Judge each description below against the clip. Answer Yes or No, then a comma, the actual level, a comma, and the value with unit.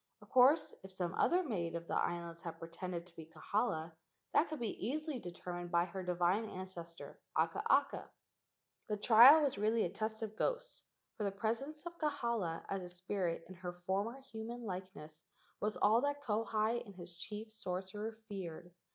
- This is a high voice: Yes, high, 200 Hz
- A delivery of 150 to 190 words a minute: Yes, average, 170 wpm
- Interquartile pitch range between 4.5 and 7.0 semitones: Yes, average, 4.9 semitones